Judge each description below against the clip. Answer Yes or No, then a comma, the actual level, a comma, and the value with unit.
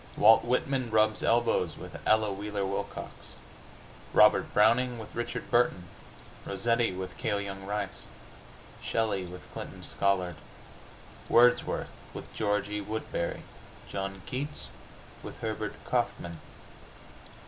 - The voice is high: No, low, 105 Hz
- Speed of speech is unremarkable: No, slow, 110 wpm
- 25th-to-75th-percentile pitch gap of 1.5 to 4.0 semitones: Yes, average, 2.9 semitones